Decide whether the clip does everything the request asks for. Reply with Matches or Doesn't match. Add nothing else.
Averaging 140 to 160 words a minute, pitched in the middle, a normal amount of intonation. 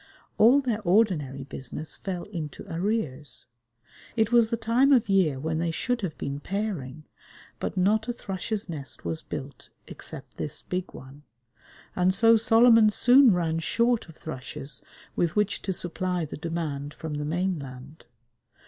Doesn't match